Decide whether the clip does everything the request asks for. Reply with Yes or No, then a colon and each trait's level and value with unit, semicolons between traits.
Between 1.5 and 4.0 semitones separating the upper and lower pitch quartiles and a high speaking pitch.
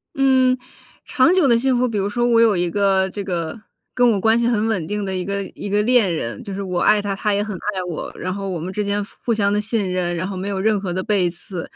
Yes: average, 3.0 semitones; high, 200 Hz